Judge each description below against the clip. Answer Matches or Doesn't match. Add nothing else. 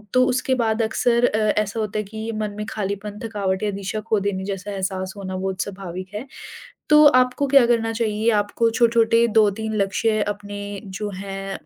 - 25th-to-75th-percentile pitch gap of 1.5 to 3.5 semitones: Matches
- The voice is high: Matches